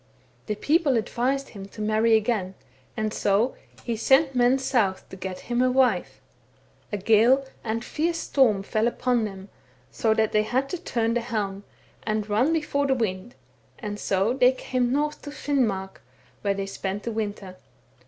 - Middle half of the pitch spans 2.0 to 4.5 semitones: Yes, average, 4.1 semitones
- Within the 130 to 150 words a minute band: No, average, 170 wpm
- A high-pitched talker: Yes, high, 225 Hz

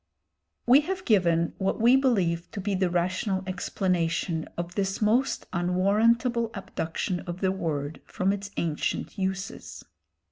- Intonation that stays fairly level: No, average, 3.4 semitones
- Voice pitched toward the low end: No, high, 190 Hz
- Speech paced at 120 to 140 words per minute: Yes, slow, 135 wpm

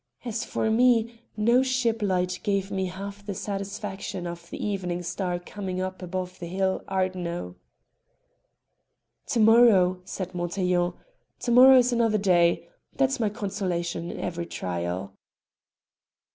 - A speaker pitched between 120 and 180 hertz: No, high, 190 Hz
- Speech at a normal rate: No, slow, 130 wpm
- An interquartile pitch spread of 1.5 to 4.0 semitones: Yes, average, 3.5 semitones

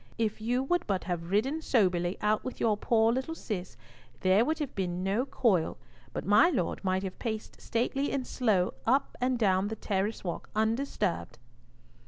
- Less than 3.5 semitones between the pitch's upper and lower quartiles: No, average, 4.9 semitones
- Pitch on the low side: No, high, 215 Hz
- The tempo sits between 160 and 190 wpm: Yes, average, 175 wpm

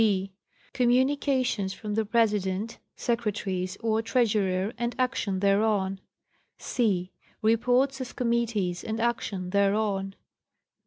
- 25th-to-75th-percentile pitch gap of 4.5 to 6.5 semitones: No, average, 3.5 semitones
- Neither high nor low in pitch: No, high, 215 Hz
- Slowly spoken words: Yes, slow, 100 wpm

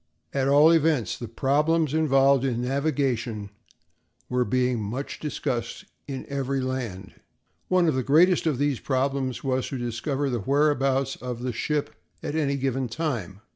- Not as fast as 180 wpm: Yes, average, 150 wpm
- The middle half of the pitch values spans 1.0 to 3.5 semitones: Yes, average, 2.7 semitones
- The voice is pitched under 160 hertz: Yes, low, 135 Hz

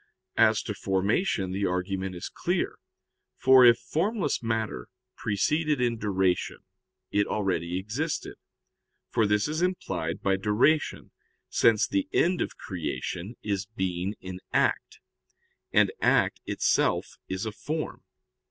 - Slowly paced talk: Yes, slow, 125 wpm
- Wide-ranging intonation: Yes, wide, 5.7 semitones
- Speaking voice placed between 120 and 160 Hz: No, low, 105 Hz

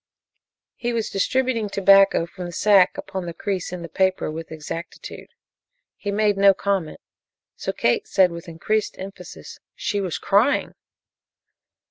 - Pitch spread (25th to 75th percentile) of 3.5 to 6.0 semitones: No, average, 2.8 semitones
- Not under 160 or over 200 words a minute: No, average, 140 wpm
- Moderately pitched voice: No, high, 195 Hz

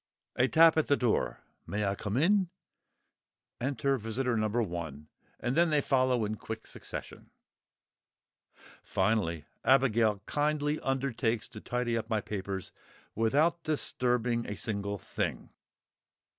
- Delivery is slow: Yes, slow, 125 wpm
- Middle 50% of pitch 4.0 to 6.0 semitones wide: Yes, average, 4.5 semitones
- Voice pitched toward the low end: Yes, low, 120 Hz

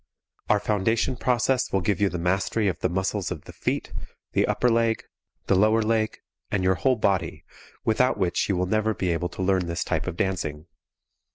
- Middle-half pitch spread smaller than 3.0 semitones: No, average, 3.4 semitones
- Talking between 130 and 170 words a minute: No, average, 195 wpm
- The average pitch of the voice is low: Yes, low, 100 Hz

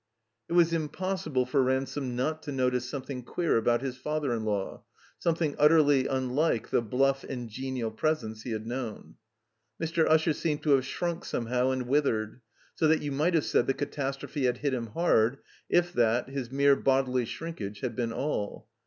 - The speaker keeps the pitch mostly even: No, average, 3.7 semitones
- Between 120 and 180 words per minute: No, average, 190 wpm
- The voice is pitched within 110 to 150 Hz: Yes, low, 135 Hz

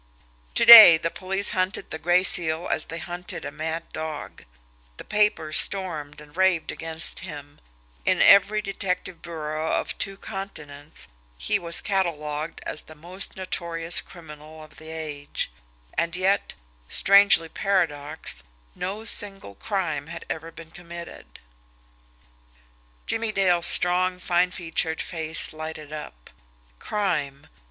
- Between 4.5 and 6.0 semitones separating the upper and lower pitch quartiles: No, average, 3.2 semitones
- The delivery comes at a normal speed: No, slow, 130 wpm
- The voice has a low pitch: No, medium, 170 Hz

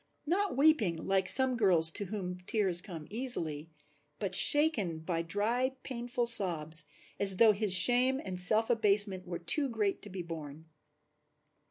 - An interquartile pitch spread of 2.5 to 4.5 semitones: No, wide, 5.5 semitones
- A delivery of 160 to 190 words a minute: No, average, 150 wpm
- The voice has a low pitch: No, high, 200 Hz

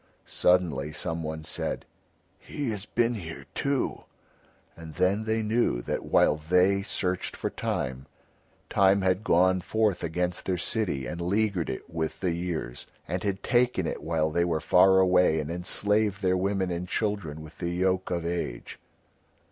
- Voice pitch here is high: No, very low, 90 Hz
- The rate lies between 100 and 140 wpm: No, average, 155 wpm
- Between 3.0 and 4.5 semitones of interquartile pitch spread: Yes, average, 3.3 semitones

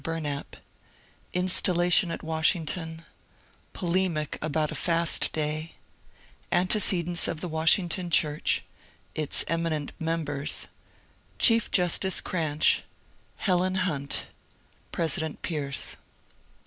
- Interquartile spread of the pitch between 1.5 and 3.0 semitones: Yes, narrow, 2.5 semitones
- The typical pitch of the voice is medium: Yes, medium, 165 Hz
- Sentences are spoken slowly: Yes, slow, 110 wpm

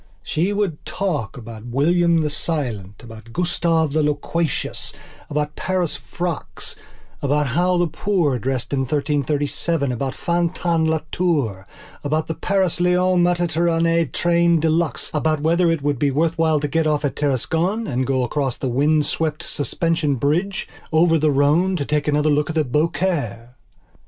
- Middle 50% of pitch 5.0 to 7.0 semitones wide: No, average, 3.3 semitones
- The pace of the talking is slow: No, average, 145 wpm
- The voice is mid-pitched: Yes, medium, 155 Hz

